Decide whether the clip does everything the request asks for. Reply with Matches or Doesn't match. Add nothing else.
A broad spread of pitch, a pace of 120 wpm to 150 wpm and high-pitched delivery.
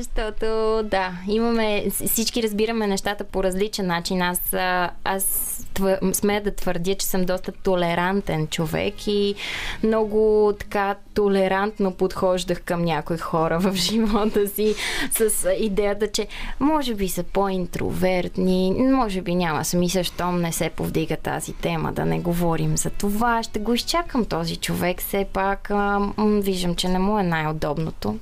Doesn't match